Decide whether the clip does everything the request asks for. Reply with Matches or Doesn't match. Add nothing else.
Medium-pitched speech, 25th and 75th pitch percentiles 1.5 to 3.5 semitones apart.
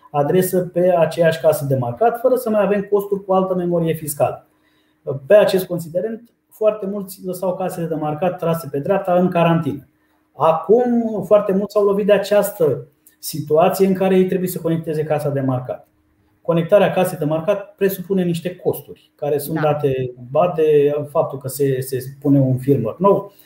Doesn't match